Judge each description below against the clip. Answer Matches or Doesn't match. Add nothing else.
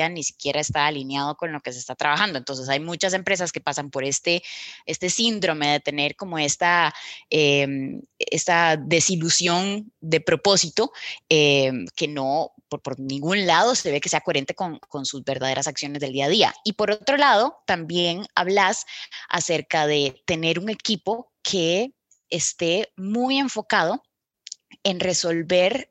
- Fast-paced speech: Doesn't match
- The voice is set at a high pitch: Doesn't match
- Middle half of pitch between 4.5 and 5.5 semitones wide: Matches